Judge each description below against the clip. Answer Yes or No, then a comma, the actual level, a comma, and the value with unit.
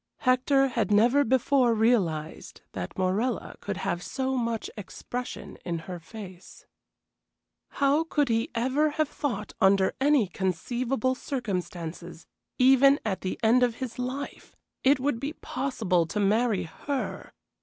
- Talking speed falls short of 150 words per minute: Yes, slow, 135 wpm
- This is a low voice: No, high, 235 Hz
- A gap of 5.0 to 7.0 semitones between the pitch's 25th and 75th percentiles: Yes, wide, 5.6 semitones